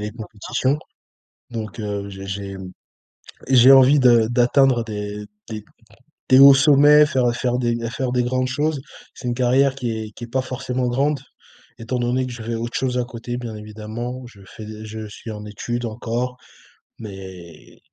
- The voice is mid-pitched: No, low, 120 Hz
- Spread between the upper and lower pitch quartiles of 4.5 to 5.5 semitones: No, average, 3.0 semitones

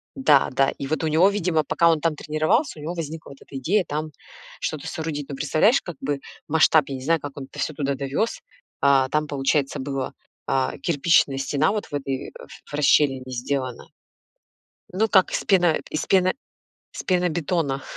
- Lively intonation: No, average, 3.4 semitones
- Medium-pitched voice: Yes, medium, 150 Hz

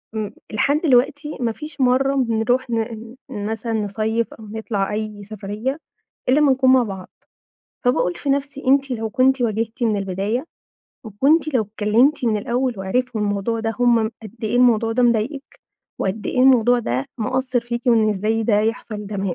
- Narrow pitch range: No, average, 3.3 semitones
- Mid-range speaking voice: No, high, 230 Hz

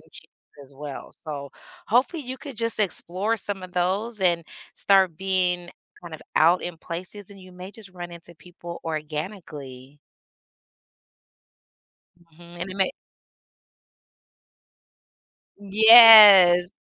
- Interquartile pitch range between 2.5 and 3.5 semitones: Yes, average, 3.2 semitones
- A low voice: No, medium, 180 Hz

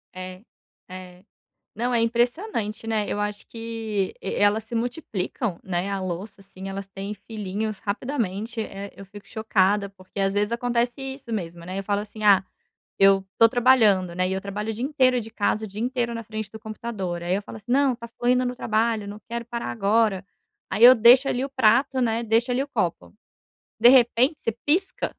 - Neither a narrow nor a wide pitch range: Yes, average, 3.3 semitones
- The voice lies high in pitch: Yes, high, 220 Hz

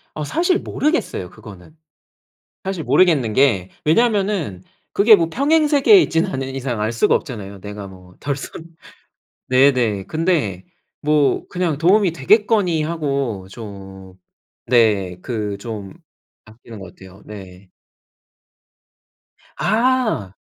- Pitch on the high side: No, low, 130 Hz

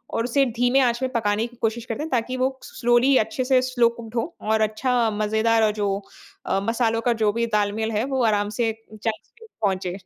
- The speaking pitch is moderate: No, high, 230 Hz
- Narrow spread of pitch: Yes, narrow, 2.3 semitones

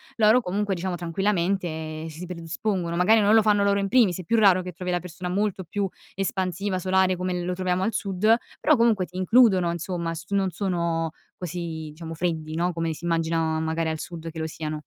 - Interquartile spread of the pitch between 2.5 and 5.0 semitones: Yes, average, 2.9 semitones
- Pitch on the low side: No, medium, 180 Hz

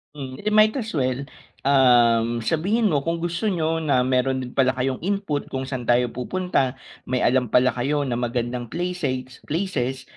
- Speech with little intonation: No, average, 4.8 semitones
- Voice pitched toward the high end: No, low, 130 Hz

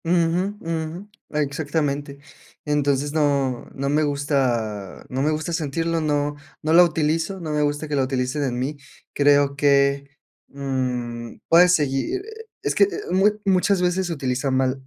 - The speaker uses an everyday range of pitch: Yes, average, 3.2 semitones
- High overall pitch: No, medium, 145 Hz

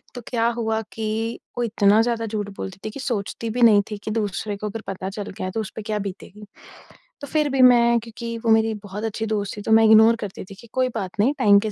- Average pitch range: No, narrow, 2.1 semitones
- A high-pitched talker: Yes, high, 220 Hz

